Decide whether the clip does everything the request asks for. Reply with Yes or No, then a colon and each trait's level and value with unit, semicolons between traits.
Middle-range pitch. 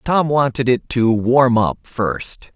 No: low, 120 Hz